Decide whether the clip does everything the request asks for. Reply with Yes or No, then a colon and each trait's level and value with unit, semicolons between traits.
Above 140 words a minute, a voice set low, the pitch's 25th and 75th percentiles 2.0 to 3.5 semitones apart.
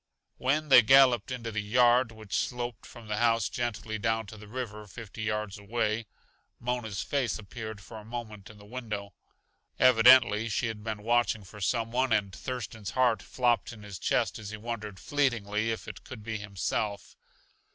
Yes: average, 175 wpm; low, 110 Hz; narrow, 2.4 semitones